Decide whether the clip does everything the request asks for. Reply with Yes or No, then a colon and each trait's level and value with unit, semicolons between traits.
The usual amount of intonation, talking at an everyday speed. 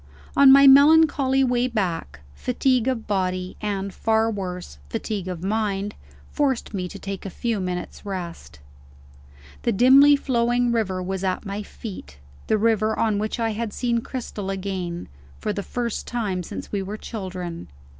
Yes: average, 4.3 semitones; average, 155 wpm